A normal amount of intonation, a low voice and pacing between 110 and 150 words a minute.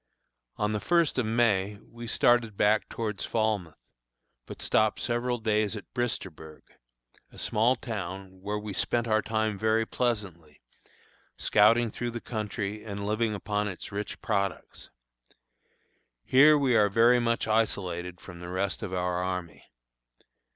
Yes: average, 3.0 semitones; low, 105 Hz; average, 140 wpm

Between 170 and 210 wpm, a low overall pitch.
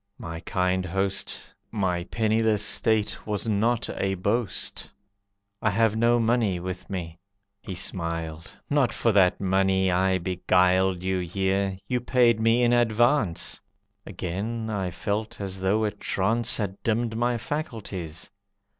No: slow, 135 wpm; low, 100 Hz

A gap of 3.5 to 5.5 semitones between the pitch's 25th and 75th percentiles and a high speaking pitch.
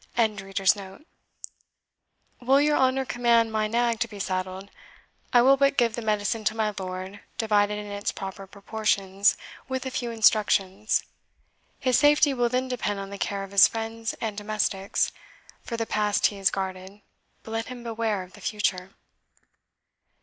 No: average, 3.1 semitones; high, 215 Hz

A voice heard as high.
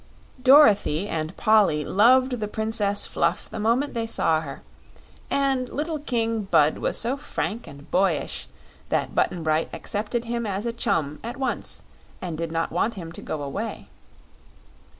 Yes: high, 210 Hz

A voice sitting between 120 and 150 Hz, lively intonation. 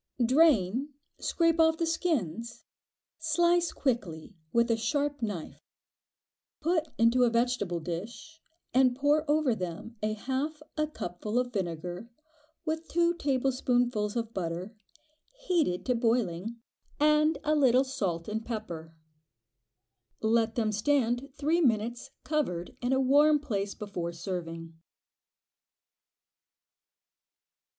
No: high, 245 Hz; wide, 6.4 semitones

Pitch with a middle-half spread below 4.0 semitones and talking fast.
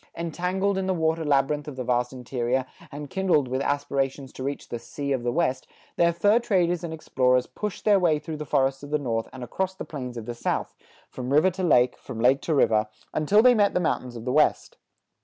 No: average, 5.3 semitones; fast, 225 wpm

